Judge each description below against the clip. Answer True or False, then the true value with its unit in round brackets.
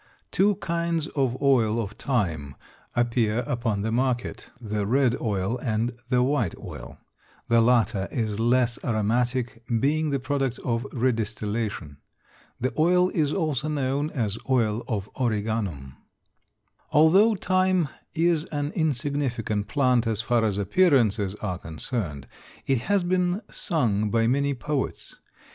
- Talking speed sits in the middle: False (130 wpm)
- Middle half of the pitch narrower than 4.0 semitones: False (4.9 semitones)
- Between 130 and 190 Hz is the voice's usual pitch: False (120 Hz)